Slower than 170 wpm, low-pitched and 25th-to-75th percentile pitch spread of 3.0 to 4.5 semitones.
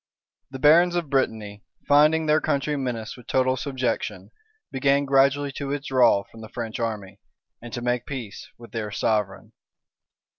Yes: average, 150 wpm; low, 130 Hz; average, 3.9 semitones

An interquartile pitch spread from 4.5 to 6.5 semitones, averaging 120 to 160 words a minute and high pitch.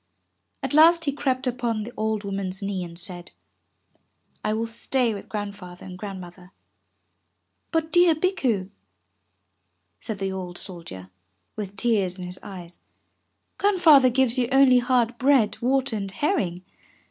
Yes: wide, 5.6 semitones; average, 140 wpm; high, 215 Hz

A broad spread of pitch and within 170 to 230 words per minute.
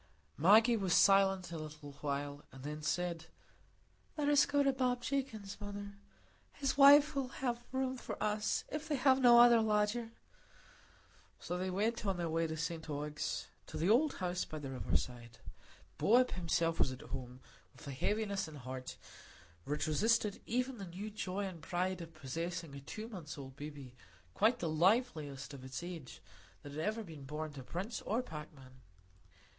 Yes: wide, 7.0 semitones; average, 175 wpm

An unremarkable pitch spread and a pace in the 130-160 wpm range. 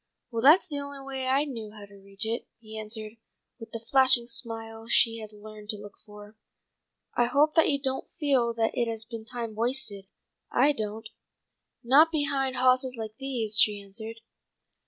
No: average, 3.6 semitones; average, 180 wpm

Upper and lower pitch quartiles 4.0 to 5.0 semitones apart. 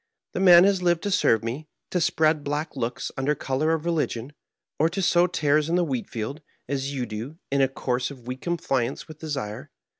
Yes: average, 4.3 semitones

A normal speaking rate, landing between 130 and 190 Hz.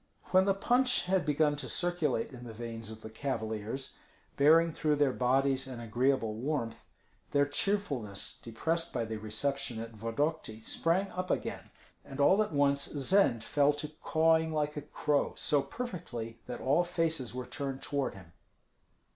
Yes: average, 160 wpm; medium, 140 Hz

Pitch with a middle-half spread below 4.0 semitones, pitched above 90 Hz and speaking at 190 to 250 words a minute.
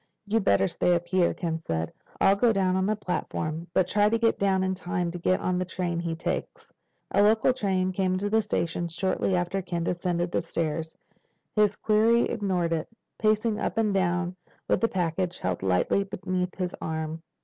Yes: average, 2.8 semitones; medium, 185 Hz; average, 195 wpm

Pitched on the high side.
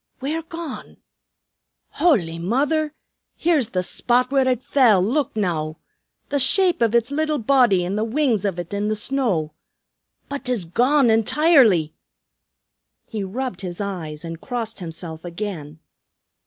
Yes: high, 225 Hz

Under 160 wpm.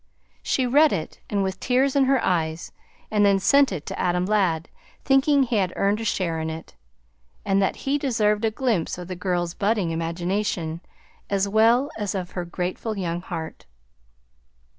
No: average, 170 wpm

